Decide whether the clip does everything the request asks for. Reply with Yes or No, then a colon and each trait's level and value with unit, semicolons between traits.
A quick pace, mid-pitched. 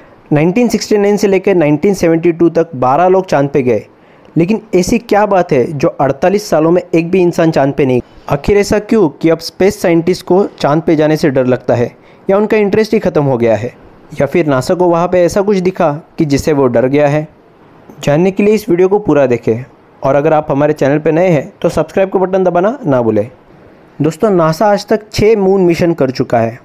Yes: fast, 220 wpm; medium, 170 Hz